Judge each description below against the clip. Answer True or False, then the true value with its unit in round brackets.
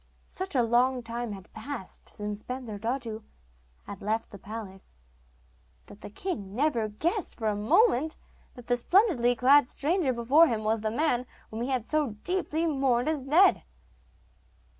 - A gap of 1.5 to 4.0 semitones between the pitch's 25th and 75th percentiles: False (5.3 semitones)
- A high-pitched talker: True (245 Hz)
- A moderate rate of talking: True (155 wpm)